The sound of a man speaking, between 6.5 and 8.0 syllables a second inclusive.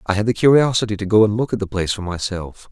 Yes: male; 7.0 syllables/s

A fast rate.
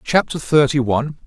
No: average, 140 wpm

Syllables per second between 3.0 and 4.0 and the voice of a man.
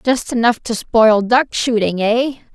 No: 3.9 syllables/s; female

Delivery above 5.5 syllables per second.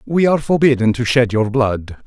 No: 5.3 syllables/s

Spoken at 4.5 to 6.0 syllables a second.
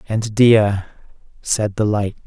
No: 3.6 syllables/s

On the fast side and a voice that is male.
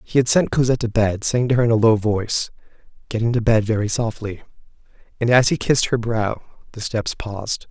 Yes: fast, 210 wpm; male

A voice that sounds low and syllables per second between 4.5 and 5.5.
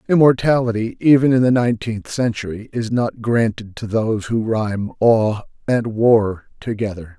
Yes: low, 115 Hz; 4.8 syllables/s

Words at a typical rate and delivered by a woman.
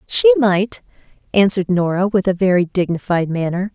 Yes: average, 145 wpm; female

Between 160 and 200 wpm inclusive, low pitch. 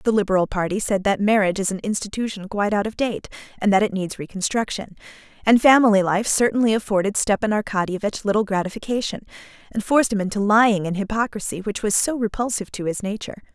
No: average, 180 wpm; high, 205 Hz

